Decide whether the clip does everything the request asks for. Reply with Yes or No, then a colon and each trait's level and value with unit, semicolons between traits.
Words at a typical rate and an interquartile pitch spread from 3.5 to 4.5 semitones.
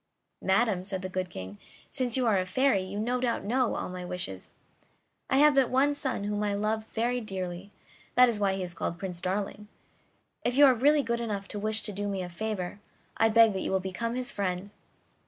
No: fast, 220 wpm; average, 4.2 semitones